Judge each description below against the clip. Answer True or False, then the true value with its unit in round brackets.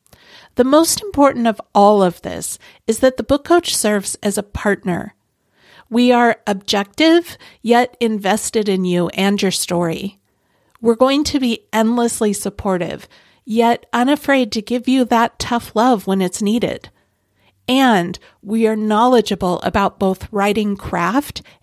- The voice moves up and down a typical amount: True (3.6 semitones)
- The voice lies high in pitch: True (220 Hz)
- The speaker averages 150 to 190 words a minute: False (140 wpm)